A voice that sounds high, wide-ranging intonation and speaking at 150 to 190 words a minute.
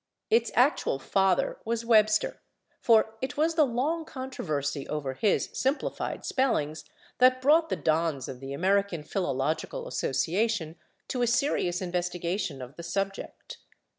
No: high, 195 Hz; wide, 8.0 semitones; slow, 135 wpm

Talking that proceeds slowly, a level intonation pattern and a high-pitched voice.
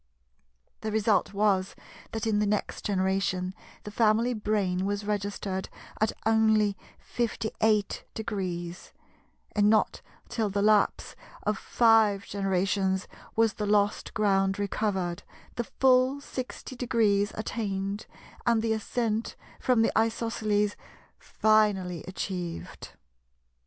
Yes: slow, 105 wpm; narrow, 2.2 semitones; high, 210 Hz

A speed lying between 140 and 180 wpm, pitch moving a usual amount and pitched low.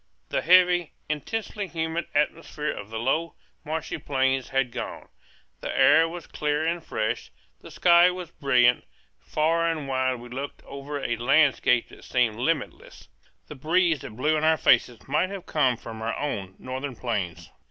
No: average, 165 wpm; average, 4.7 semitones; medium, 145 Hz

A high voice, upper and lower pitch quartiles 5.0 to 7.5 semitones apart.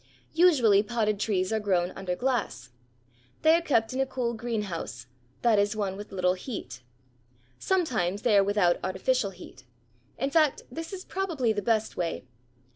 Yes: high, 215 Hz; wide, 5.4 semitones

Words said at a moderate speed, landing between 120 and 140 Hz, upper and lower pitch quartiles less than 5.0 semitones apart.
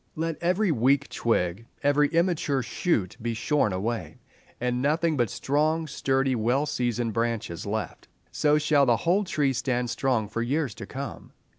Yes: average, 155 wpm; low, 135 Hz; average, 4.5 semitones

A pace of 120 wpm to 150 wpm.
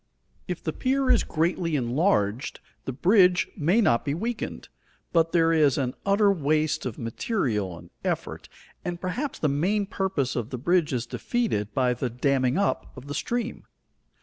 No: average, 165 wpm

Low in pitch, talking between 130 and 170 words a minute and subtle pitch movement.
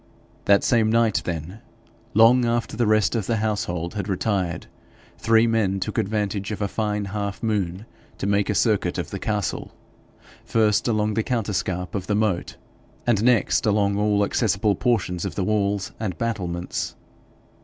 Yes: low, 105 Hz; average, 160 wpm; narrow, 2.3 semitones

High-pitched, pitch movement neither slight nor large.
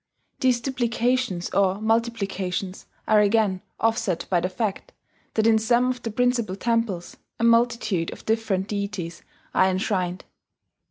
Yes: high, 215 Hz; average, 3.7 semitones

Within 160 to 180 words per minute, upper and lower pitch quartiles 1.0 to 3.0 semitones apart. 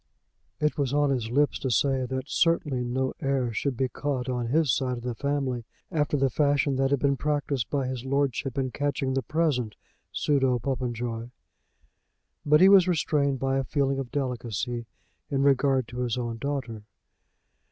Yes: average, 175 wpm; narrow, 2.4 semitones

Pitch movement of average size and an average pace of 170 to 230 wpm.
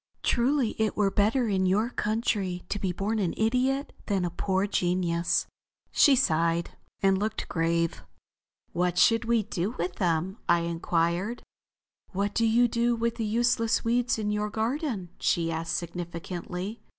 No: average, 4.6 semitones; average, 150 wpm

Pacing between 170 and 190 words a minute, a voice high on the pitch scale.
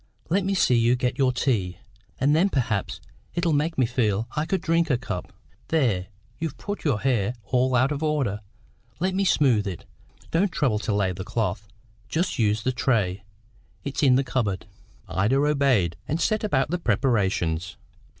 No: average, 175 wpm; low, 130 Hz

